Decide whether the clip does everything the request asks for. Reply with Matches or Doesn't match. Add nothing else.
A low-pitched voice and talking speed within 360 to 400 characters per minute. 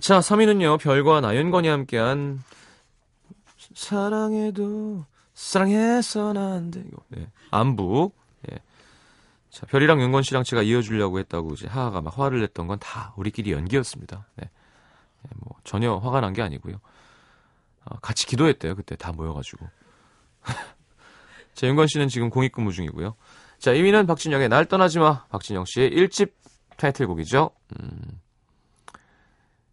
Doesn't match